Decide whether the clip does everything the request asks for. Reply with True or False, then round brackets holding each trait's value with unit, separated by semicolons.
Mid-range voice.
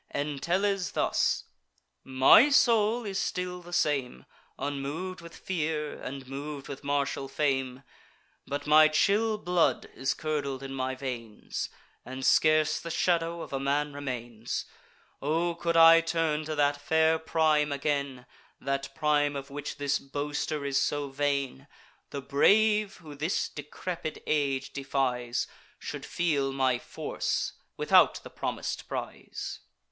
True (145 Hz)